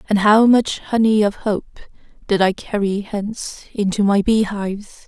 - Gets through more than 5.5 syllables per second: No, 4.6 syllables/s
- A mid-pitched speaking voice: No, high, 210 Hz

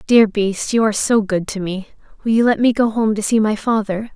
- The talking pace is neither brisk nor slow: No, fast, 260 wpm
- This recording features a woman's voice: Yes, female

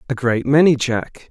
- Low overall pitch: Yes, low, 130 Hz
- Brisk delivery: No, average, 185 wpm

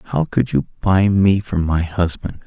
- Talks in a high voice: No, very low, 95 Hz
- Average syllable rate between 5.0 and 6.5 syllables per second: No, 4.0 syllables/s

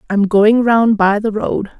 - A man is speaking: No, female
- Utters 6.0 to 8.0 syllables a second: No, 4.0 syllables/s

